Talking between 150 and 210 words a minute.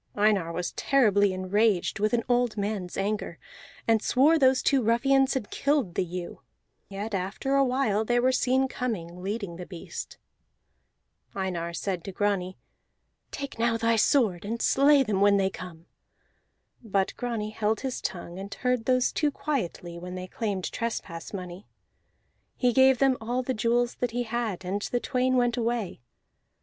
Yes: average, 160 wpm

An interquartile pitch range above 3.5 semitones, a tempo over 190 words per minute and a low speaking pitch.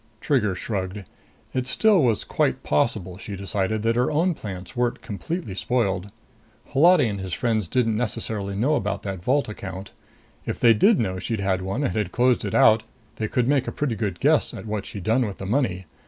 Yes: average, 4.3 semitones; average, 200 wpm; low, 110 Hz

